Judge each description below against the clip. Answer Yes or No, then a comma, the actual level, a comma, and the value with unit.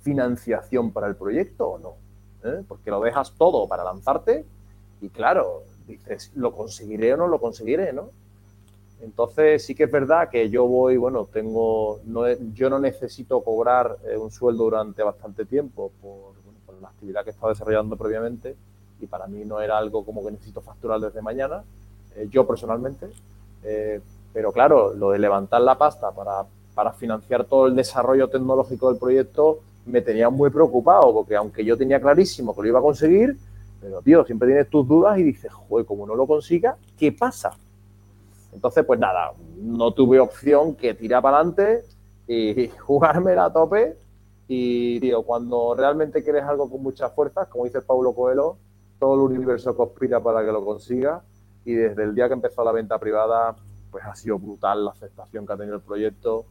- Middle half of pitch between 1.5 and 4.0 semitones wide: No, average, 4.5 semitones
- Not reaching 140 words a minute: No, average, 180 wpm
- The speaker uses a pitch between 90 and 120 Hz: Yes, low, 115 Hz